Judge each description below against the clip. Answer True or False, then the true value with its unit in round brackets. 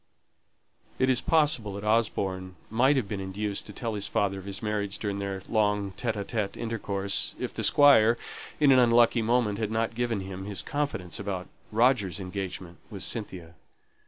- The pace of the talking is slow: False (165 wpm)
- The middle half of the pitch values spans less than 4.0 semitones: True (3.1 semitones)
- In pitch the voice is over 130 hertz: False (105 Hz)